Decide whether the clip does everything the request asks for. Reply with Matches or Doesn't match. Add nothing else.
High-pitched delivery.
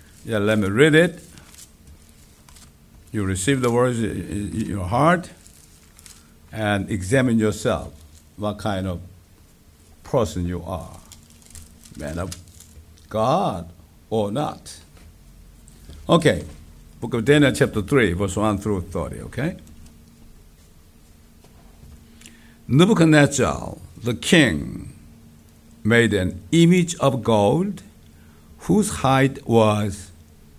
Doesn't match